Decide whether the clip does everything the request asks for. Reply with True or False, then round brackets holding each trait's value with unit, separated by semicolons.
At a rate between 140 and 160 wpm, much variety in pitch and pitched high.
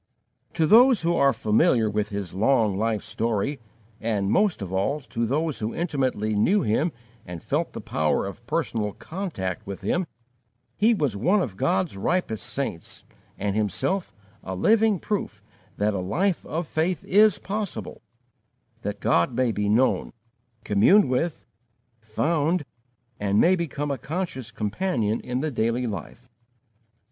False (145 wpm; 8.6 semitones; 125 Hz)